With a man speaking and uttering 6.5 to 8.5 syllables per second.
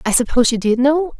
No: female; 6.7 syllables/s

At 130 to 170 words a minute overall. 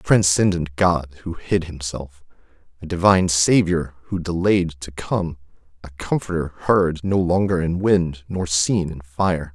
Yes: average, 150 wpm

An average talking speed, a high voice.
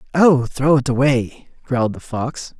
No: average, 160 wpm; low, 135 Hz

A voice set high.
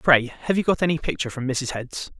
No: medium, 140 Hz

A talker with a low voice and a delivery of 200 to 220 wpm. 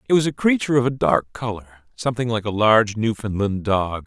Yes: low, 110 Hz; fast, 205 wpm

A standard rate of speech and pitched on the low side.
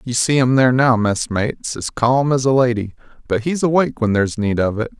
No: fast, 230 wpm; low, 120 Hz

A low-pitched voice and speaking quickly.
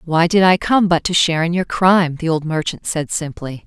No: medium, 170 Hz; fast, 245 wpm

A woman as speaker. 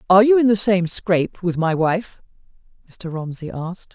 Yes: female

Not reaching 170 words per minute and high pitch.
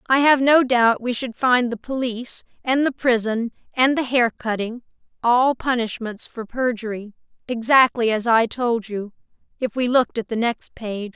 Yes: average, 160 wpm; high, 240 Hz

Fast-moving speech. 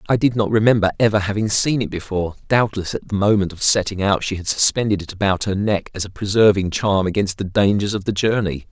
Yes: fast, 225 wpm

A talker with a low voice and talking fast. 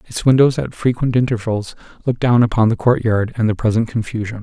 No: low, 115 Hz; average, 190 wpm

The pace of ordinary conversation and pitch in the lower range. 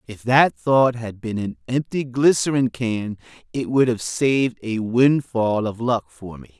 Yes: average, 175 wpm; low, 120 Hz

